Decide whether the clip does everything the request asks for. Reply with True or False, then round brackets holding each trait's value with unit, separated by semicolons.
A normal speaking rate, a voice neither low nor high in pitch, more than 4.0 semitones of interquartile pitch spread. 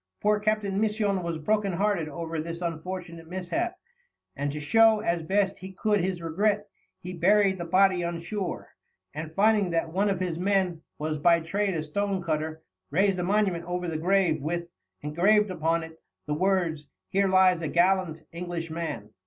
False (170 wpm; 180 Hz; 3.2 semitones)